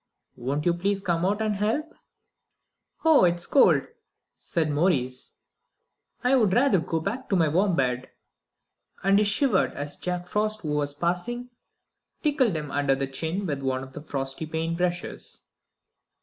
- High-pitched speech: No, medium, 175 Hz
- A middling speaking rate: Yes, average, 155 wpm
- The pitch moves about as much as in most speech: No, wide, 6.1 semitones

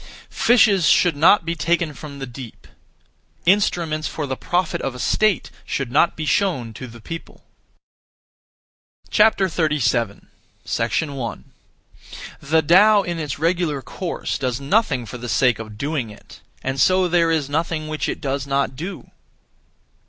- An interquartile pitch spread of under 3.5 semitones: No, average, 4.6 semitones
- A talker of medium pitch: Yes, medium, 155 Hz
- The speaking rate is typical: Yes, average, 145 wpm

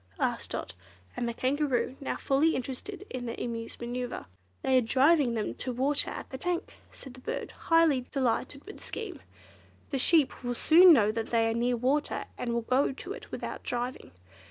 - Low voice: No, very high, 260 Hz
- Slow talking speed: No, average, 190 wpm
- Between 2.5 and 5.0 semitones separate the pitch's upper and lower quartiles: Yes, average, 3.6 semitones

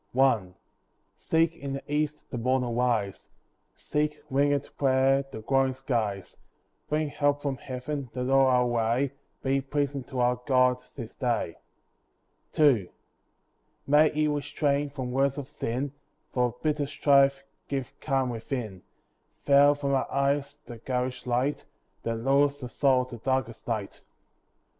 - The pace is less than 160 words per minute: Yes, average, 140 wpm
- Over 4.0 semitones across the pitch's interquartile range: No, narrow, 2.4 semitones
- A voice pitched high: No, low, 135 Hz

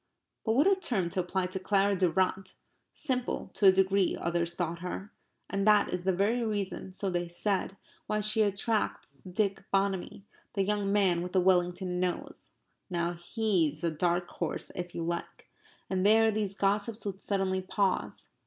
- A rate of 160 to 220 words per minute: Yes, average, 170 wpm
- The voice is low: No, high, 190 Hz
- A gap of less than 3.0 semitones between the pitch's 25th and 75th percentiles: Yes, narrow, 2.5 semitones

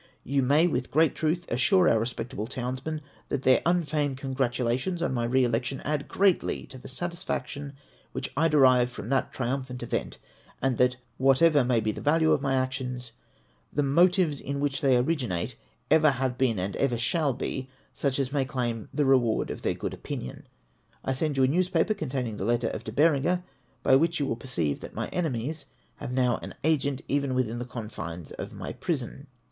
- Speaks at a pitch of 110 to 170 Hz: Yes, low, 135 Hz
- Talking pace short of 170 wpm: No, average, 190 wpm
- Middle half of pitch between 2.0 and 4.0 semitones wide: Yes, average, 3.4 semitones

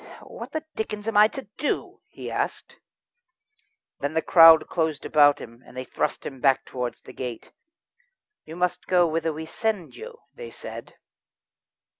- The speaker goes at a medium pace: Yes, average, 155 wpm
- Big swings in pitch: Yes, wide, 6.5 semitones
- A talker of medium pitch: Yes, medium, 165 Hz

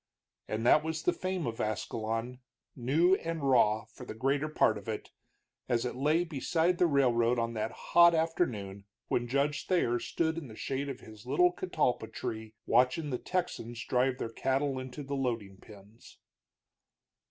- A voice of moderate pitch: No, low, 130 Hz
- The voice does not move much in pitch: No, average, 5.3 semitones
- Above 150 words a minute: Yes, average, 165 wpm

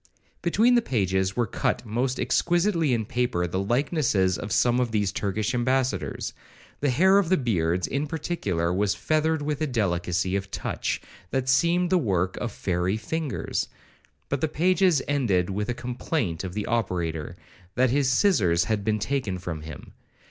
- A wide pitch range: Yes, wide, 7.4 semitones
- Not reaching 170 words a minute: Yes, average, 160 wpm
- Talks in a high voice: No, low, 120 Hz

